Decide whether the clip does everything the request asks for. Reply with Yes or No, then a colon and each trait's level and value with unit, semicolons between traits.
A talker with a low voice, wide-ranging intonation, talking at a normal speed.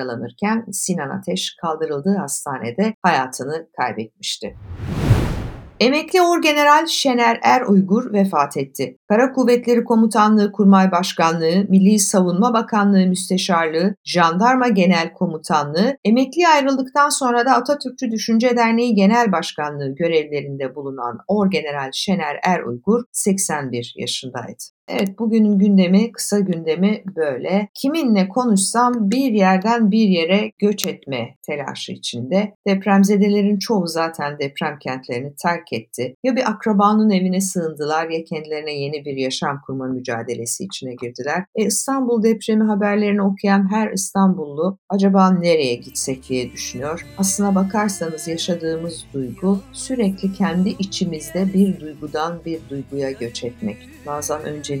No: high, 190 Hz; wide, 5.8 semitones; average, 115 wpm